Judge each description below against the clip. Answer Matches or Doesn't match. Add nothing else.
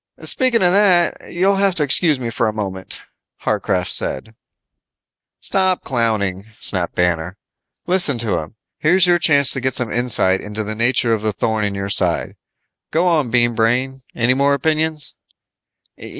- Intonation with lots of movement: Matches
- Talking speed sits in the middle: Matches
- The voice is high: Doesn't match